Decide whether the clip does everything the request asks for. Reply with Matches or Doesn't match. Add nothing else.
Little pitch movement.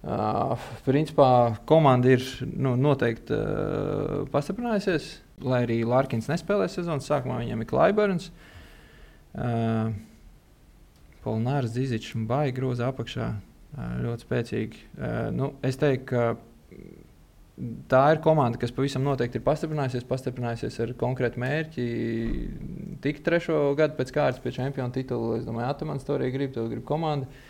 Doesn't match